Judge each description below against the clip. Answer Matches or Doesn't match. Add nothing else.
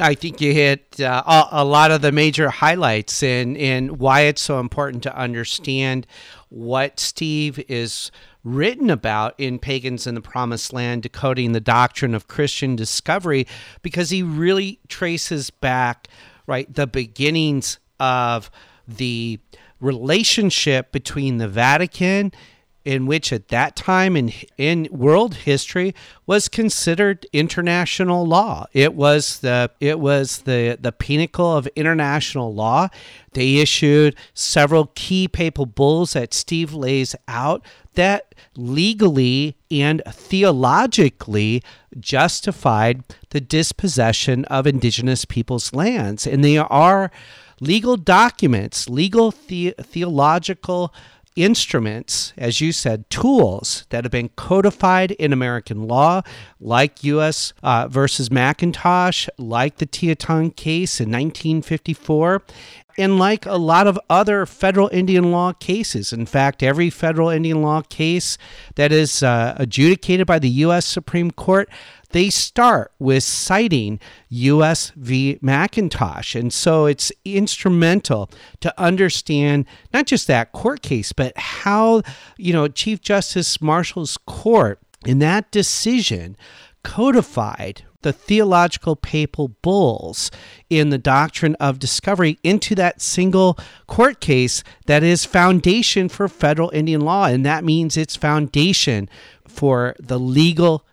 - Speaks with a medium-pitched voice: Matches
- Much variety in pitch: Matches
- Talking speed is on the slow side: Matches